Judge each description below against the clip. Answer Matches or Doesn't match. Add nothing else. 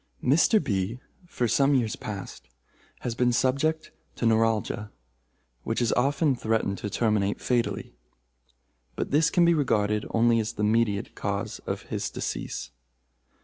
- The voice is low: Matches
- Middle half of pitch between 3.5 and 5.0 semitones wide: Matches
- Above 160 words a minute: Doesn't match